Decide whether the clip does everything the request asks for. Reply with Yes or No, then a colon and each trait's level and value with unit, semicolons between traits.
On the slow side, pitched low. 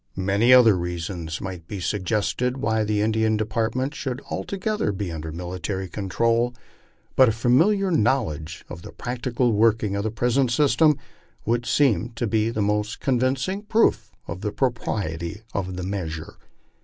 No: average, 155 wpm; low, 110 Hz